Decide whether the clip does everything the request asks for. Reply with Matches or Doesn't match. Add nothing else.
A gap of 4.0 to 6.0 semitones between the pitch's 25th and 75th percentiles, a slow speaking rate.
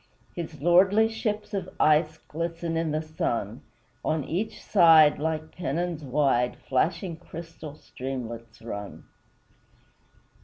Doesn't match